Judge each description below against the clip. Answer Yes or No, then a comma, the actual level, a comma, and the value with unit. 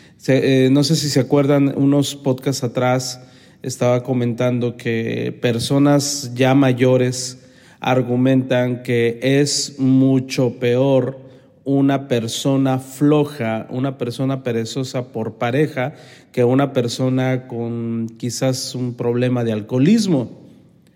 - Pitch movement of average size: No, narrow, 1.8 semitones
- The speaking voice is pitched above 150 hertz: No, low, 130 Hz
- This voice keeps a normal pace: No, slow, 105 wpm